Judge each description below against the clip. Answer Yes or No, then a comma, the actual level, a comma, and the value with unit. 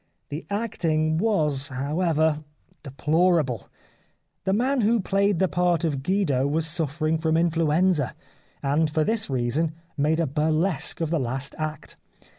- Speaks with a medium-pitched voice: Yes, medium, 160 Hz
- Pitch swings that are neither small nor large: Yes, average, 3.3 semitones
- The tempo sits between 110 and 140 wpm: Yes, slow, 135 wpm